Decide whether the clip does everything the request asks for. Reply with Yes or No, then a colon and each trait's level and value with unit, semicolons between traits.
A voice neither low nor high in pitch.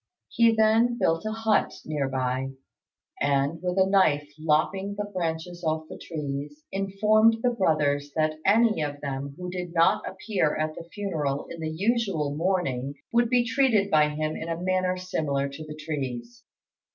Yes: medium, 165 Hz